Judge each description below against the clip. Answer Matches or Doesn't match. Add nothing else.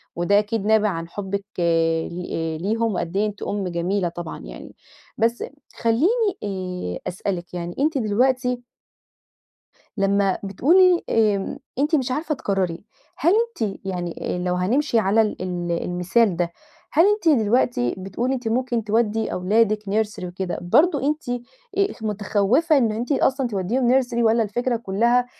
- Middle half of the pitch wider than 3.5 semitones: Matches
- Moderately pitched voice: Doesn't match